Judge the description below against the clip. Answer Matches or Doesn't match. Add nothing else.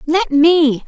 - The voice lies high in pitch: Matches